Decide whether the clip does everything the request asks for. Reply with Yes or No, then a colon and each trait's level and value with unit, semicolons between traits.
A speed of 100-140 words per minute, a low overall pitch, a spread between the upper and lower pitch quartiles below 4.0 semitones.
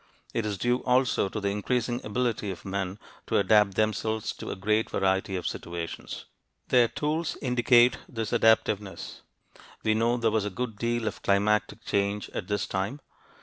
No: average, 165 wpm; low, 110 Hz; average, 3.2 semitones